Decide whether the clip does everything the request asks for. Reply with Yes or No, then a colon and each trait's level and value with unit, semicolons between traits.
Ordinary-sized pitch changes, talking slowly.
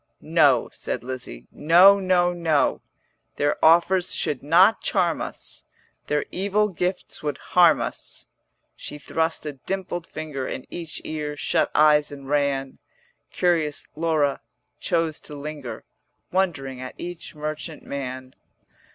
Yes: average, 3.5 semitones; slow, 125 wpm